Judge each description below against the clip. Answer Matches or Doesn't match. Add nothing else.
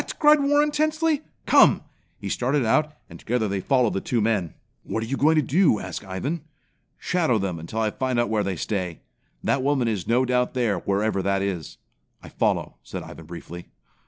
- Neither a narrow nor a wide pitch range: Doesn't match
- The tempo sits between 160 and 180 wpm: Doesn't match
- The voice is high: Doesn't match